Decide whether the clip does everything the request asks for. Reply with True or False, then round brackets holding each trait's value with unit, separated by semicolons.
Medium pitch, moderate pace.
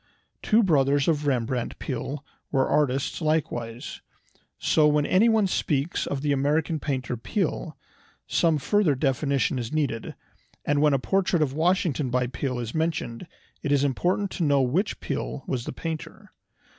True (145 Hz; 150 wpm)